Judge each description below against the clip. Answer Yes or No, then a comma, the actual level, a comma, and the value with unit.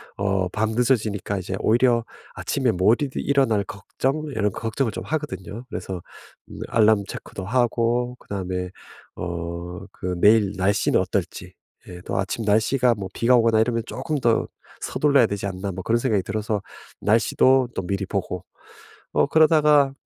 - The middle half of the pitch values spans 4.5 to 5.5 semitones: No, average, 4.1 semitones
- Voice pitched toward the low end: Yes, low, 110 Hz